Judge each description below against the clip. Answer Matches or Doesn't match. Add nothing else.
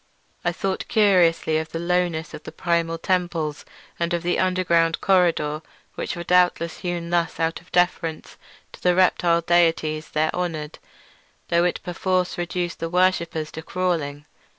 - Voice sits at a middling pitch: Matches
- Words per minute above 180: Doesn't match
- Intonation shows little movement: Matches